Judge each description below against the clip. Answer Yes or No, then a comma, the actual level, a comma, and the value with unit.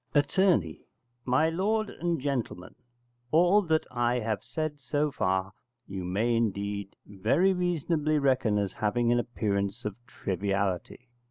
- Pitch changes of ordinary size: No, wide, 7.3 semitones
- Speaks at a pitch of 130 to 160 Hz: No, low, 120 Hz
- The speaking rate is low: Yes, slow, 125 wpm